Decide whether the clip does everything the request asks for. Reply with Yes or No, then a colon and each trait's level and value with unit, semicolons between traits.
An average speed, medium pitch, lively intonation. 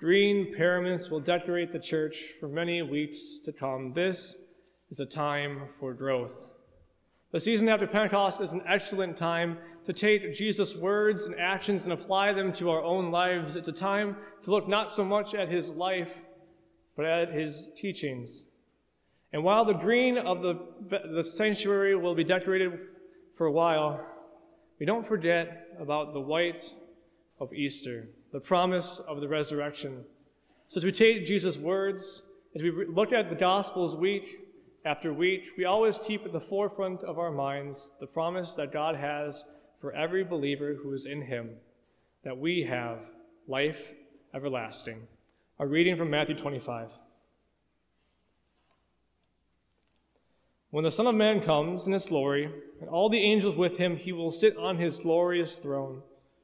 No: average, 155 wpm; medium, 175 Hz; average, 4.7 semitones